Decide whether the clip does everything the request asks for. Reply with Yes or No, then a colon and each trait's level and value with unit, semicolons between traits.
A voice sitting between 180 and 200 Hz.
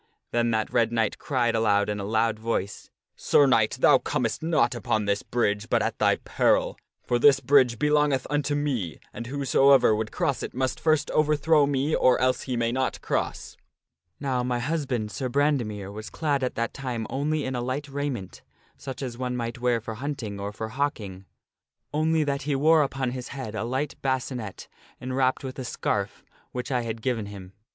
No: low, 125 Hz